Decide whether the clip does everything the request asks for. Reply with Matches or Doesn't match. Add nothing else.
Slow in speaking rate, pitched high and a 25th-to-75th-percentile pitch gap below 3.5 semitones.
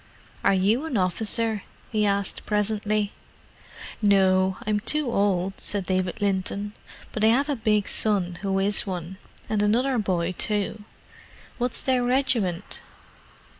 Matches